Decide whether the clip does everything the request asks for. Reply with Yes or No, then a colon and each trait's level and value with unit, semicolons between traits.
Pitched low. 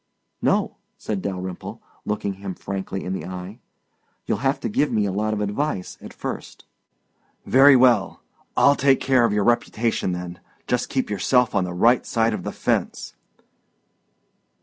Yes: low, 105 Hz